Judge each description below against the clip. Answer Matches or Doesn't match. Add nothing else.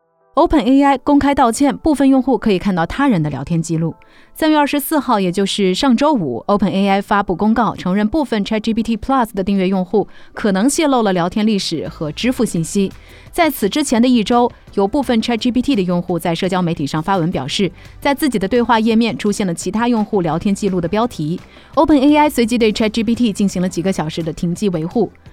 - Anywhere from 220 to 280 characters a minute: Doesn't match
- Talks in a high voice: Matches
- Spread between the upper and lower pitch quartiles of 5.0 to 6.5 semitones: Matches